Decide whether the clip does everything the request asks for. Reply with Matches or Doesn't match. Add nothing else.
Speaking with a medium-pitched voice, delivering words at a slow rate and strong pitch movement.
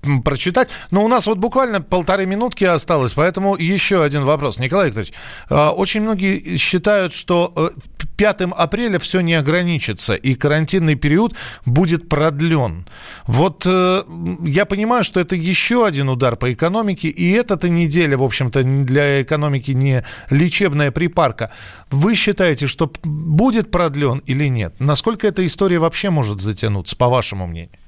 Doesn't match